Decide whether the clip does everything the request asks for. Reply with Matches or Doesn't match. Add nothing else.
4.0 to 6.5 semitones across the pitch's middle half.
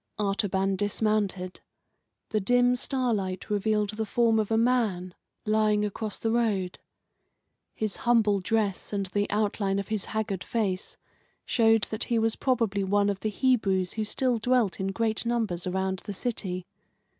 Doesn't match